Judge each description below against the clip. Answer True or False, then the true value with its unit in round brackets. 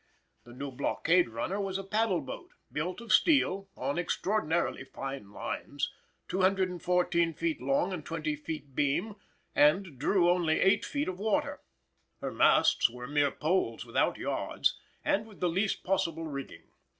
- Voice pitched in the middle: True (170 Hz)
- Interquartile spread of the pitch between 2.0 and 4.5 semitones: False (5.0 semitones)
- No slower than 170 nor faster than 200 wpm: False (150 wpm)